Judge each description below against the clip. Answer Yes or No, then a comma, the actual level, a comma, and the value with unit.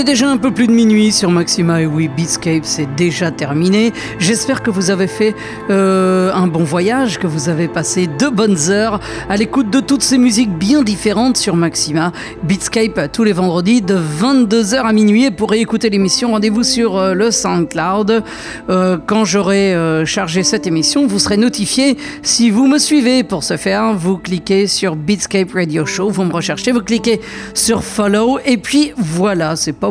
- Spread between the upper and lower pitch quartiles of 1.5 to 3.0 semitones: No, average, 4.3 semitones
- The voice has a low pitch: No, high, 205 Hz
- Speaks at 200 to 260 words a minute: No, average, 185 wpm